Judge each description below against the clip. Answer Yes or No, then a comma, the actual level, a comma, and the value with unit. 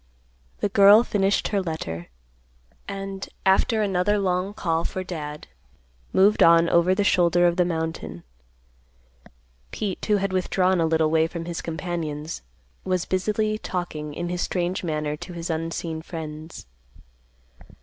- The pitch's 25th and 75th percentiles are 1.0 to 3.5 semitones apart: Yes, average, 2.9 semitones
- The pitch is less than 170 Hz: No, medium, 175 Hz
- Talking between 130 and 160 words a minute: Yes, average, 140 wpm